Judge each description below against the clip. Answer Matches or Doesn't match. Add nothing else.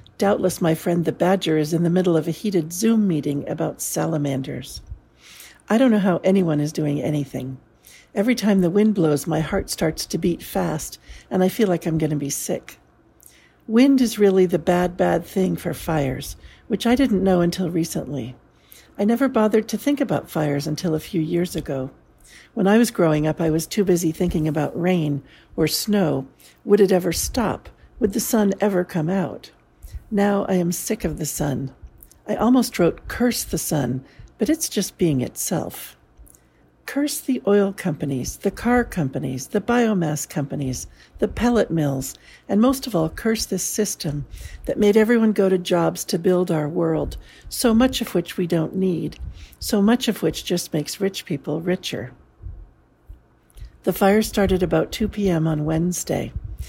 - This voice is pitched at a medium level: Matches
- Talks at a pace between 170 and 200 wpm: Matches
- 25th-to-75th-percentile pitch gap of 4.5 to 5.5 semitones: Matches